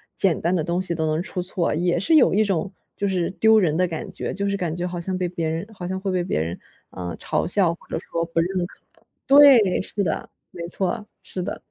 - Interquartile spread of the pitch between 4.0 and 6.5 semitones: No, narrow, 2.5 semitones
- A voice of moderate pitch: Yes, medium, 180 Hz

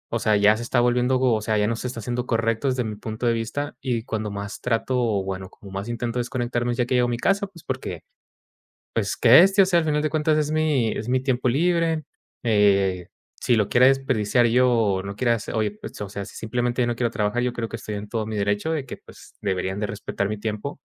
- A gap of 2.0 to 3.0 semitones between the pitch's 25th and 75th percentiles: No, average, 3.4 semitones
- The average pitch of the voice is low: Yes, low, 120 Hz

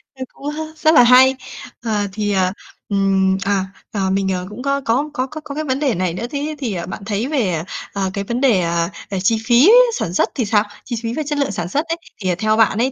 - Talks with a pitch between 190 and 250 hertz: Yes, high, 220 Hz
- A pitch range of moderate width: No, wide, 5.8 semitones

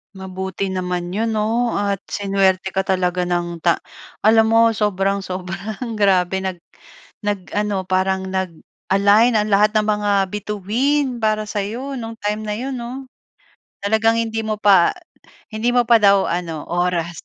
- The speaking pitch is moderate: No, high, 205 Hz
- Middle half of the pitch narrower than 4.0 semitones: Yes, average, 2.8 semitones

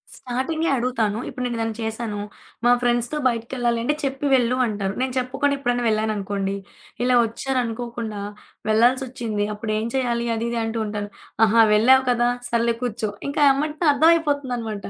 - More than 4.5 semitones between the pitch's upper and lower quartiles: No, average, 2.8 semitones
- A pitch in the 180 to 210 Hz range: No, high, 235 Hz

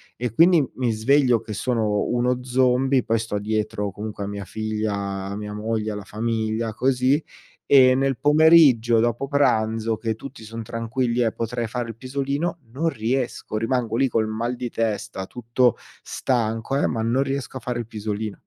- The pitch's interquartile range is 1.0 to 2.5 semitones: No, average, 2.9 semitones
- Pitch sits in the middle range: No, low, 115 Hz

